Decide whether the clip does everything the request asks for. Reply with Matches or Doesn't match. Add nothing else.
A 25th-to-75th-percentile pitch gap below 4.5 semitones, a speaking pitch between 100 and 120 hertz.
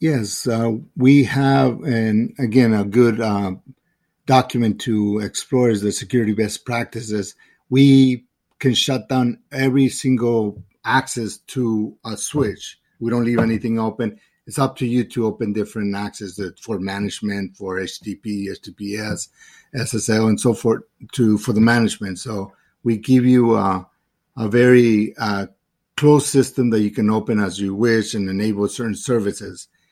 Matches